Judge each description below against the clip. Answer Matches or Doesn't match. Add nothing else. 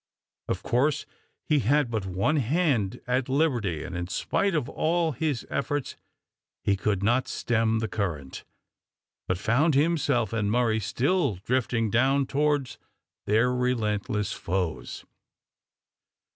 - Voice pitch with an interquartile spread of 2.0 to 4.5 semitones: Doesn't match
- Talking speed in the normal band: Doesn't match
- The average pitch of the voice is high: Doesn't match